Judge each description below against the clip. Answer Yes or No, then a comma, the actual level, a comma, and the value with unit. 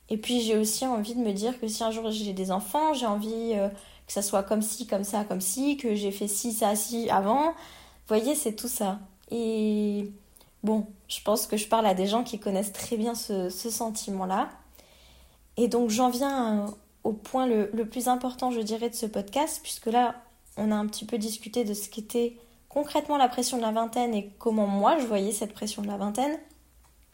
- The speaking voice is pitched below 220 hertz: No, high, 225 Hz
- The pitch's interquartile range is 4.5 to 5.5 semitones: No, narrow, 2.6 semitones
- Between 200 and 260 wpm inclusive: Yes, fast, 220 wpm